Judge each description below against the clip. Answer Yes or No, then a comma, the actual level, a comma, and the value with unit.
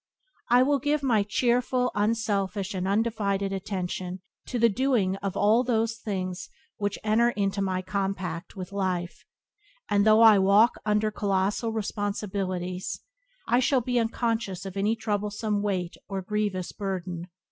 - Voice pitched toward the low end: No, high, 205 Hz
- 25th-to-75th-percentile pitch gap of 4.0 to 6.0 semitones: No, average, 2.9 semitones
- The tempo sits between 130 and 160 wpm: Yes, average, 140 wpm